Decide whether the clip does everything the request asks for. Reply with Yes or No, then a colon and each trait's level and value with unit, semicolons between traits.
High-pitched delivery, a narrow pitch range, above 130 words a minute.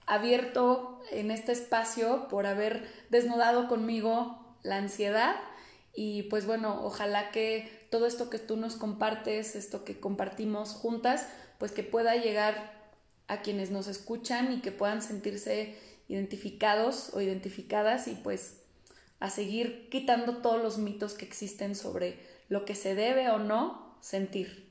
Yes: high, 215 Hz; narrow, 2.3 semitones; average, 140 wpm